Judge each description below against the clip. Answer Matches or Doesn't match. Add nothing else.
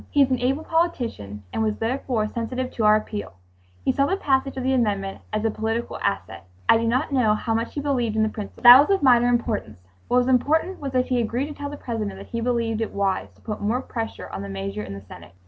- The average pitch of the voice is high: Matches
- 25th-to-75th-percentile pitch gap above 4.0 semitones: Doesn't match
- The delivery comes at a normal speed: Doesn't match